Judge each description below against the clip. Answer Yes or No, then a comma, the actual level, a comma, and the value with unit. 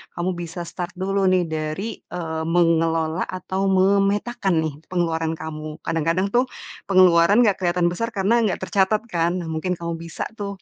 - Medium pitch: Yes, medium, 175 Hz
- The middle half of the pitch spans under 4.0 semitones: Yes, average, 2.8 semitones